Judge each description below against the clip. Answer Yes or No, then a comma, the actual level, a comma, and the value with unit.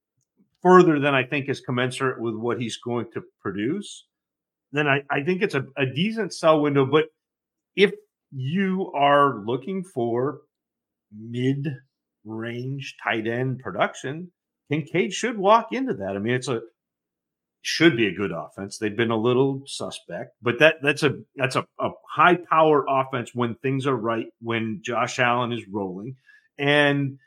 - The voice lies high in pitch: No, low, 135 Hz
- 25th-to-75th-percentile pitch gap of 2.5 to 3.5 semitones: No, average, 4.7 semitones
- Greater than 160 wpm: No, average, 155 wpm